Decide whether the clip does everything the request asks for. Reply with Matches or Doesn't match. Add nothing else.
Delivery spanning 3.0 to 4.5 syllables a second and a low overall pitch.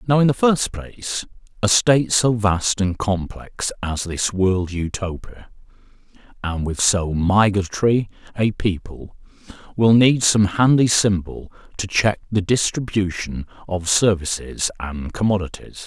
Matches